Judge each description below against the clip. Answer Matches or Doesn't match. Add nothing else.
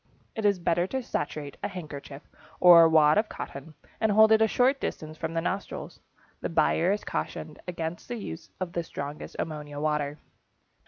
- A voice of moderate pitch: Matches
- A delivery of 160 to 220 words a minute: Matches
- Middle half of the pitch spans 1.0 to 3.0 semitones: Doesn't match